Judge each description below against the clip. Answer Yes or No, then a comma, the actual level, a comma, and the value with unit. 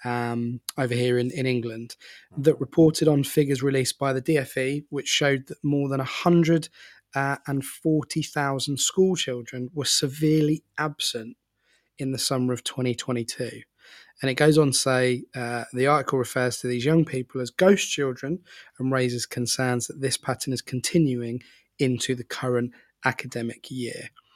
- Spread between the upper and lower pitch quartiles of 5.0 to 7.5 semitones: No, average, 3.0 semitones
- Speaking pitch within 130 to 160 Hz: Yes, low, 135 Hz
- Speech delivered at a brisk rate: No, average, 150 wpm